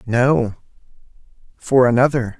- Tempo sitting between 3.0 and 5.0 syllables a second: Yes, 3.7 syllables/s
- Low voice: Yes, low, 125 Hz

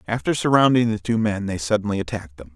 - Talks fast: Yes, fast, 210 wpm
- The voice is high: No, low, 105 Hz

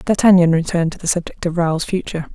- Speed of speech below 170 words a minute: No, fast, 205 wpm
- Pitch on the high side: No, medium, 170 Hz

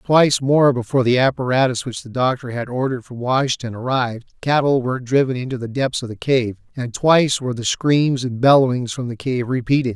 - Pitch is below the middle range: Yes, low, 125 Hz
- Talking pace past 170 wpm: Yes, average, 200 wpm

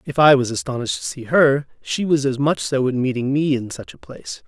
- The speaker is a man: Yes, male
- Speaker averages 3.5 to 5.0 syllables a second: No, 5.7 syllables/s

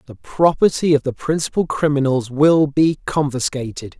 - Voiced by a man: Yes, male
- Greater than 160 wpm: No, slow, 135 wpm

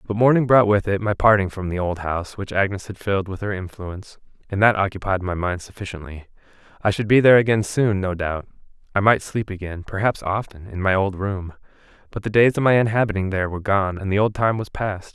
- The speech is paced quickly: Yes, fast, 220 wpm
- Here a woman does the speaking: No, male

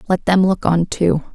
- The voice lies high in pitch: No, medium, 175 Hz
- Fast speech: Yes, fast, 220 wpm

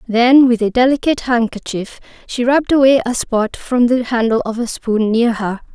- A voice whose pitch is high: Yes, high, 240 Hz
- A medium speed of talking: Yes, average, 190 wpm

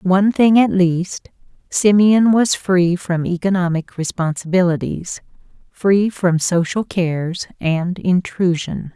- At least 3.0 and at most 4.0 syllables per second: Yes, 3.8 syllables/s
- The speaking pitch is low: No, medium, 180 Hz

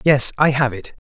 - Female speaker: No, male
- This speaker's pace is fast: Yes, fast, 225 wpm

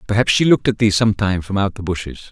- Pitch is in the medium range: No, low, 100 Hz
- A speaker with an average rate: No, fast, 260 wpm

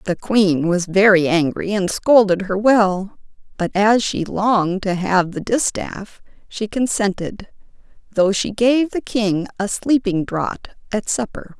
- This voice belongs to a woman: Yes, female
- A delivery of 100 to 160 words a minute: Yes, average, 150 wpm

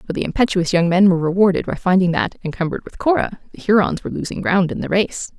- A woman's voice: Yes, female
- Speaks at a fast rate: Yes, fast, 235 wpm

